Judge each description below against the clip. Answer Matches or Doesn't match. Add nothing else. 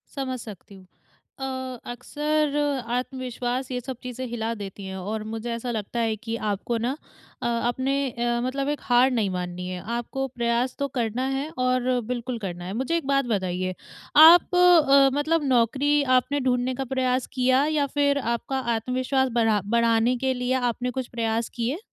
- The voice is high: Matches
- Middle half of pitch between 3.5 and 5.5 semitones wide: Doesn't match